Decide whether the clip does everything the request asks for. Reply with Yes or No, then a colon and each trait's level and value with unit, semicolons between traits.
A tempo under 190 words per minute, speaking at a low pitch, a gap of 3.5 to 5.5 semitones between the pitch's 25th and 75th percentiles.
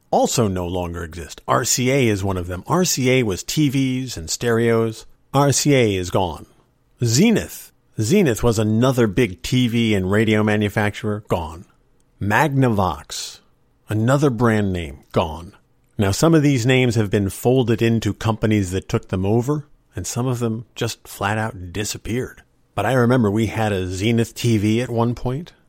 Yes: average, 150 wpm; low, 115 Hz; average, 3.9 semitones